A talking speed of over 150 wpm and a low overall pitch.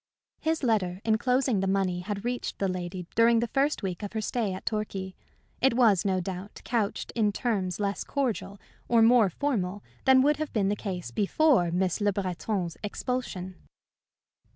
No: average, 170 wpm; high, 205 Hz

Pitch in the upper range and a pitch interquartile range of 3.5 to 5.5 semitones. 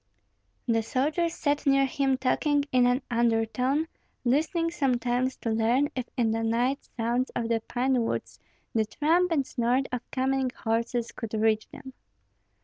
No: very high, 255 Hz; average, 3.1 semitones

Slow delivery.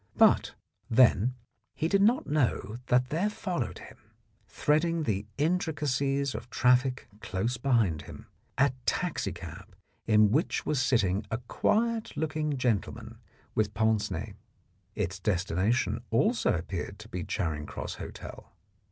Yes: slow, 130 wpm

